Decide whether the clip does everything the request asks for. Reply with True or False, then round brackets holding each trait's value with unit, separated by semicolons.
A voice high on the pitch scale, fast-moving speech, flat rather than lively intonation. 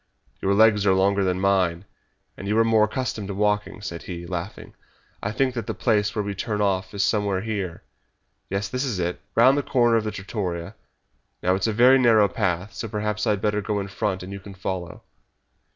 False (100 Hz; 215 wpm; 2.3 semitones)